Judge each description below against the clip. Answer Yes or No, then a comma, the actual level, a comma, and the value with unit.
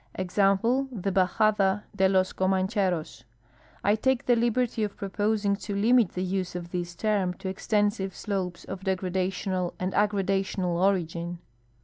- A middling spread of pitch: No, narrow, 2.2 semitones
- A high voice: Yes, high, 195 Hz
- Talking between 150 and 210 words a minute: No, slow, 135 wpm